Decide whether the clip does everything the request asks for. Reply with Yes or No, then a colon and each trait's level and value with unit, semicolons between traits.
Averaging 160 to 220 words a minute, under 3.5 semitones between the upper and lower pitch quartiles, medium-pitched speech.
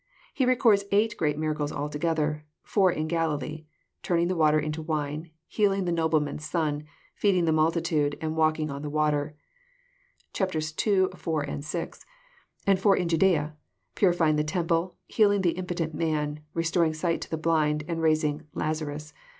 Yes: average, 165 wpm; narrow, 2.5 semitones; medium, 160 Hz